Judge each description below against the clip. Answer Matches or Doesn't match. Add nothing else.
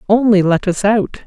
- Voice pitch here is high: Matches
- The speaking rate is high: Doesn't match